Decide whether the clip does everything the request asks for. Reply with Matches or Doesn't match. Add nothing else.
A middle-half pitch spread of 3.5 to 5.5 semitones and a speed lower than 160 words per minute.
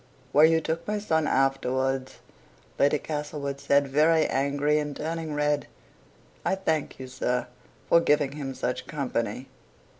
Doesn't match